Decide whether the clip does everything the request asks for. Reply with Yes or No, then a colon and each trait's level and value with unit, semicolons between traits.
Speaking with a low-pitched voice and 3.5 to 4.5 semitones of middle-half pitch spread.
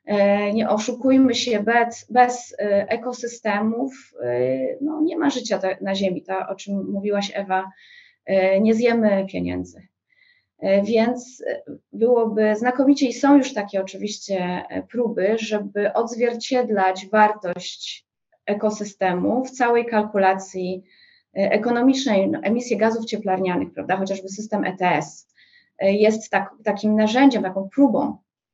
No: high, 215 Hz; average, 4.0 semitones